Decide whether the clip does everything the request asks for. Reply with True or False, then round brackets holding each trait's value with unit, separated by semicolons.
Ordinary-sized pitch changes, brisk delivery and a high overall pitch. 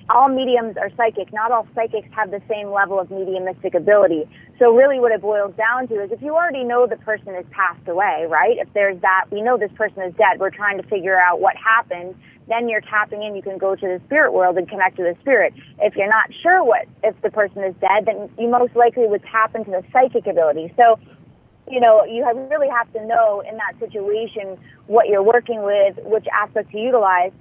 True (3.4 semitones; 225 wpm; 215 Hz)